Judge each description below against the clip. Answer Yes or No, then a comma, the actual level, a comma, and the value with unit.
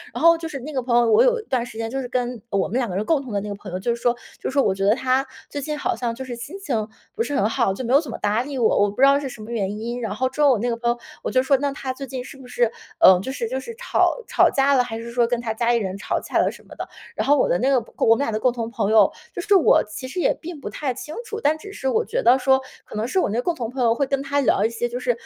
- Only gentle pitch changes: No, average, 3.5 semitones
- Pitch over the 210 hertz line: Yes, very high, 250 Hz